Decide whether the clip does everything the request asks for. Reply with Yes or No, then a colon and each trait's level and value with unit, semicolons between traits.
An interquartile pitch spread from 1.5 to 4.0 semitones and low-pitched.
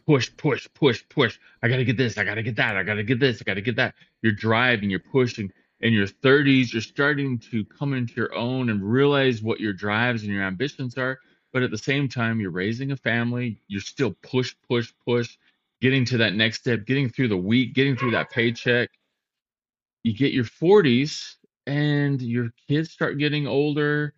Yes: average, 3.3 semitones; low, 125 Hz